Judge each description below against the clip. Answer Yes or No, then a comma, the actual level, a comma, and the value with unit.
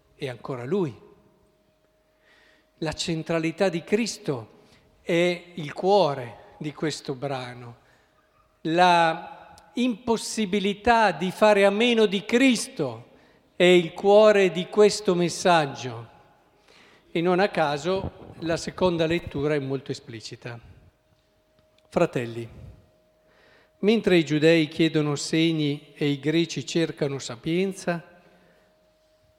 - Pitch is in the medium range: Yes, medium, 165 Hz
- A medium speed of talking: No, slow, 100 wpm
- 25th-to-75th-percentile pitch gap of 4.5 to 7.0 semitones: Yes, wide, 5.4 semitones